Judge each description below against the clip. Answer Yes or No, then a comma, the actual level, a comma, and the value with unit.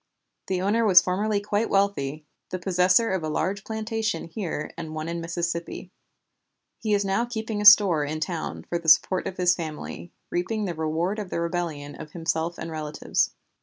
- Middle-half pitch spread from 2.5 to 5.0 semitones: Yes, average, 4.1 semitones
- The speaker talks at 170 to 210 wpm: Yes, average, 180 wpm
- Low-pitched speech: No, medium, 180 Hz